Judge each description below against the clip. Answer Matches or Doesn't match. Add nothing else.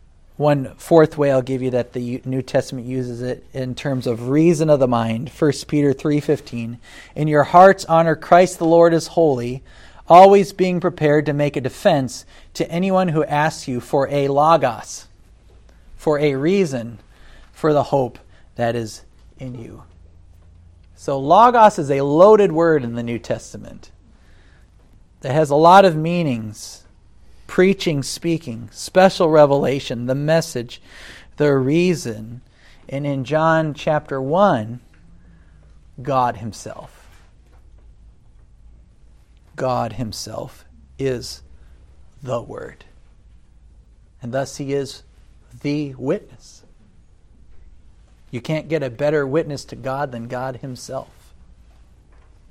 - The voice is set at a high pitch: Doesn't match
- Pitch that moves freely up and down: Matches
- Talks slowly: Matches